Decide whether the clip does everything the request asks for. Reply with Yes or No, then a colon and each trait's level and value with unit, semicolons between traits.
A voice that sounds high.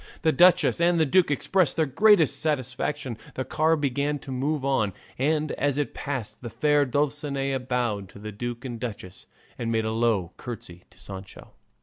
No: low, 135 Hz